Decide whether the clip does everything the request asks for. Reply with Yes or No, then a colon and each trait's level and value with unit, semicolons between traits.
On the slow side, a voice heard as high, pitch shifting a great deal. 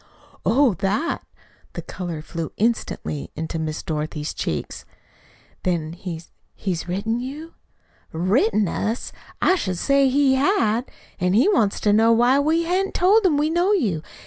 No: average, 145 wpm; high, 225 Hz; wide, 8.5 semitones